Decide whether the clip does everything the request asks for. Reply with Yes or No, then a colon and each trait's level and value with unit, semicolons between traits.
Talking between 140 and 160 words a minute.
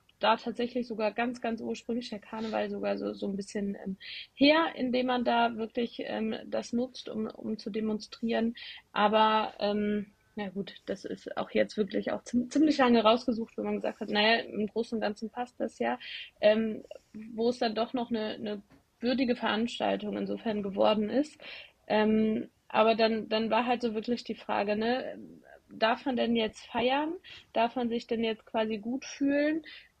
No: average, 175 wpm